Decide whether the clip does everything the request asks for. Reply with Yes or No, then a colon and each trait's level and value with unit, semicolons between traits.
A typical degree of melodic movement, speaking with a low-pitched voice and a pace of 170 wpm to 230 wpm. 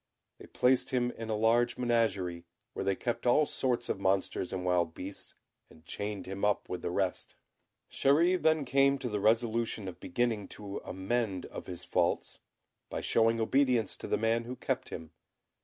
Yes: average, 4.2 semitones; low, 110 Hz; average, 175 wpm